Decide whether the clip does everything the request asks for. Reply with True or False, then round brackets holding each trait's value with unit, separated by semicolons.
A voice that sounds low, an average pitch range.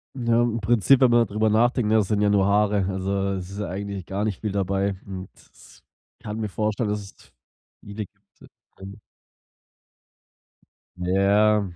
False (105 Hz; 1.8 semitones)